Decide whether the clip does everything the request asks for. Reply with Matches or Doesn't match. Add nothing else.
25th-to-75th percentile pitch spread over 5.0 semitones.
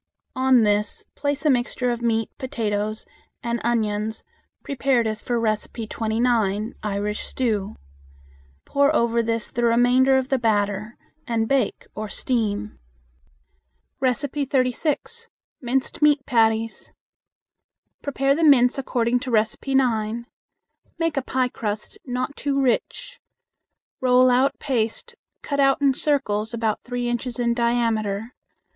Doesn't match